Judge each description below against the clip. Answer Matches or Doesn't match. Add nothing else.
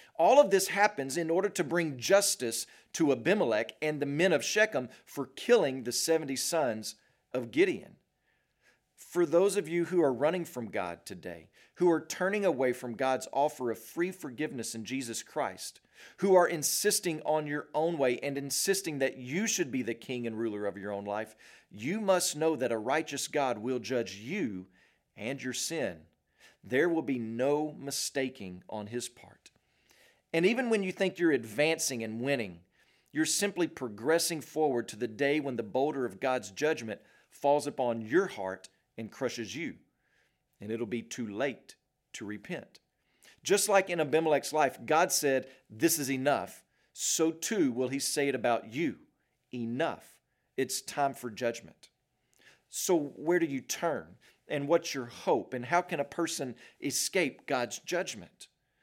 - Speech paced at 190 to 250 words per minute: Doesn't match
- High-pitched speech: Doesn't match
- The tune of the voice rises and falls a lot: Matches